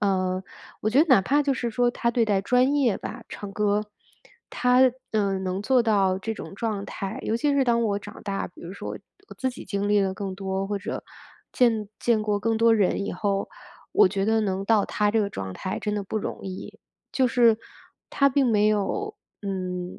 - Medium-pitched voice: No, high, 210 Hz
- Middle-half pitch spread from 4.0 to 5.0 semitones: No, average, 3.3 semitones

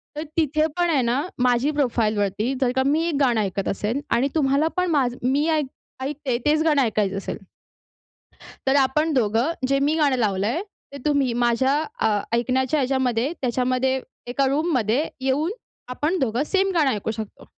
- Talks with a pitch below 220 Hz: No, very high, 265 Hz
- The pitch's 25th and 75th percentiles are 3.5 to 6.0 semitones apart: Yes, average, 3.9 semitones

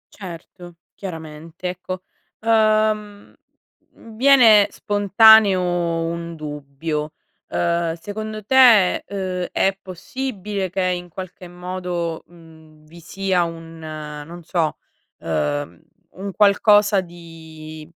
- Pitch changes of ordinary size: Yes, average, 3.8 semitones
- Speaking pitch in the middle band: Yes, medium, 180 Hz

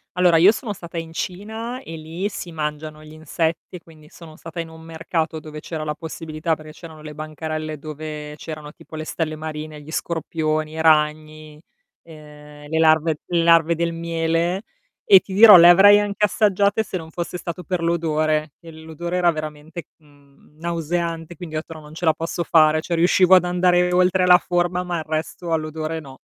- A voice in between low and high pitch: Yes, medium, 160 Hz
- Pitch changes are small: Yes, narrow, 2.0 semitones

